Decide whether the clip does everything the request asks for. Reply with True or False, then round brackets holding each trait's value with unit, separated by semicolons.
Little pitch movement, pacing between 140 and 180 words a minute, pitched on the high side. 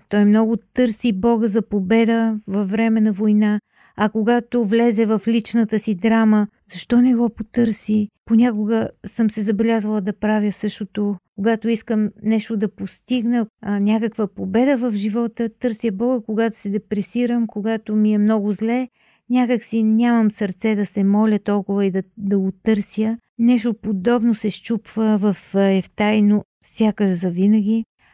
True (1.7 semitones; 145 wpm; 220 Hz)